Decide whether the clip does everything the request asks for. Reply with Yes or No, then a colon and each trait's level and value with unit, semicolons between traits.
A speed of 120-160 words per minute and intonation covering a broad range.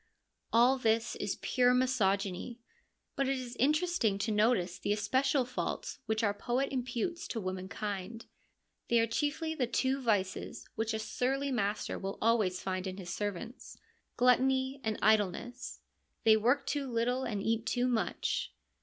No: average, 150 wpm; average, 3.9 semitones